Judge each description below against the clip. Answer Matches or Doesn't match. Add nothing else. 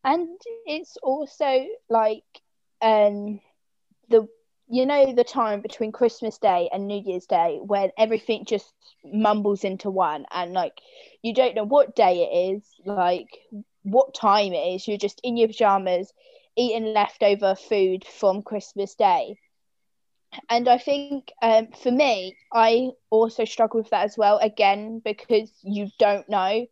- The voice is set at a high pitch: Matches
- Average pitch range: Matches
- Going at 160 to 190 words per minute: Doesn't match